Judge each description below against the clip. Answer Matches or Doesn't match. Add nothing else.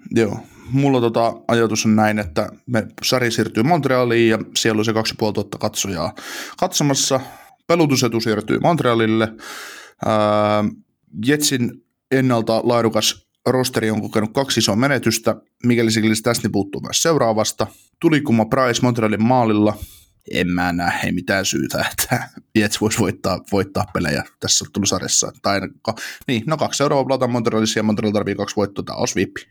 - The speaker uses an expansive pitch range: Doesn't match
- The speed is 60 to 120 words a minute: Doesn't match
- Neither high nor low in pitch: Doesn't match